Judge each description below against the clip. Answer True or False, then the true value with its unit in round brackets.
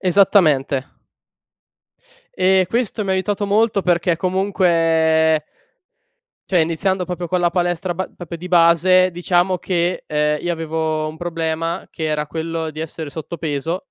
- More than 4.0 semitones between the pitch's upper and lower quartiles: False (2.5 semitones)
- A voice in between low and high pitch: True (170 Hz)